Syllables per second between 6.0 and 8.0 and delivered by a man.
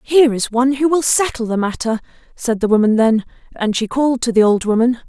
No: 6.1 syllables/s; female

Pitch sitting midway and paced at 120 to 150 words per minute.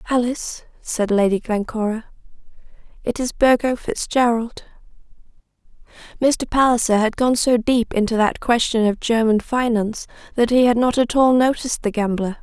No: high, 235 Hz; average, 140 wpm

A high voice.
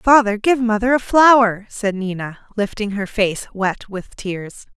Yes: high, 215 Hz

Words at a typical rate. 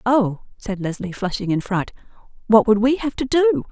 Yes: average, 195 wpm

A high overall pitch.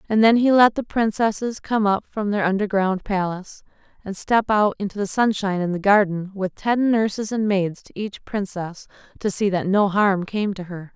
Yes: high, 200 Hz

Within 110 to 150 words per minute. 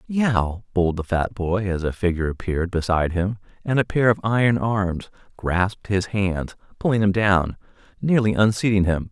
No: average, 170 wpm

